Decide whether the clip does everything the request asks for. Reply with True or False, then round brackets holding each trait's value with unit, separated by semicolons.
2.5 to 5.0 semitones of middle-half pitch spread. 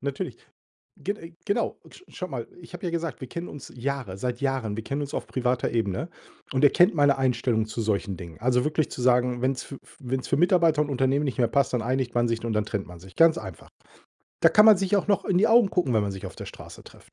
False (5.4 semitones)